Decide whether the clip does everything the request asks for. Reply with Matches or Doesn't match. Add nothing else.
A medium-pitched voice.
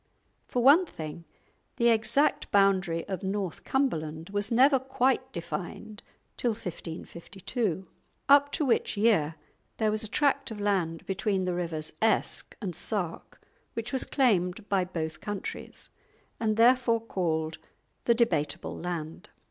Doesn't match